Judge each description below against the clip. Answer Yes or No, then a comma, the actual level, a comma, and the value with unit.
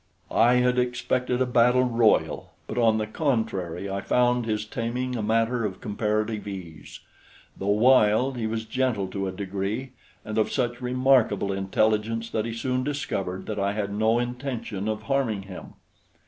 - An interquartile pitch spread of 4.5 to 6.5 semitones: No, average, 3.3 semitones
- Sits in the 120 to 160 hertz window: No, low, 110 Hz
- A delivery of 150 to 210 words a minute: Yes, average, 160 wpm